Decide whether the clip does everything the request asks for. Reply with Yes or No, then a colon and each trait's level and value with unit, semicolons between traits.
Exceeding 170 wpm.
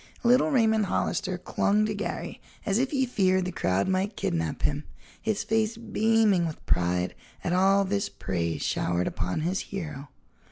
No: average, 160 wpm